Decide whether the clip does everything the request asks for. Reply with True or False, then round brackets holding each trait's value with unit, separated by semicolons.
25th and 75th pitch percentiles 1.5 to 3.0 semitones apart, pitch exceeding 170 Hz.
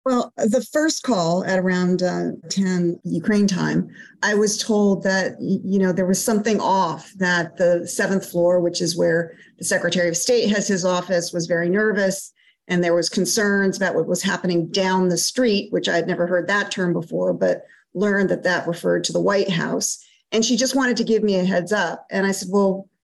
True (2.7 semitones; 190 Hz)